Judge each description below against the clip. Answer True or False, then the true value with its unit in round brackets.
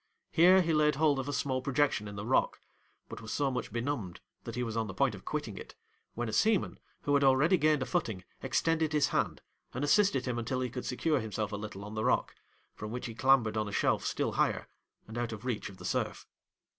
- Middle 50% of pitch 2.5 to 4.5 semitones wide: False (4.9 semitones)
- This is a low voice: True (125 Hz)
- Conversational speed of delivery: False (240 wpm)